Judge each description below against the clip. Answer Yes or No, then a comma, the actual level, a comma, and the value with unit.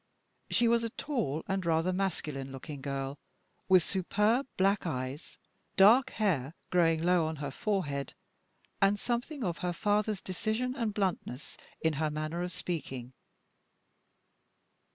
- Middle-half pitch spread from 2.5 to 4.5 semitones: No, wide, 5.5 semitones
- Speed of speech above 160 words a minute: No, slow, 135 wpm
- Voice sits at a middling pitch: Yes, medium, 180 Hz